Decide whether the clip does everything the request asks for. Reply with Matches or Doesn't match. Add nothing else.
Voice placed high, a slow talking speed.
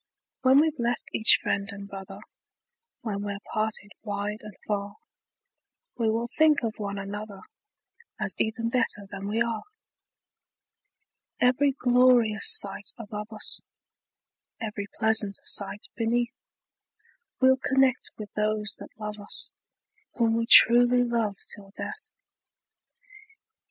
Matches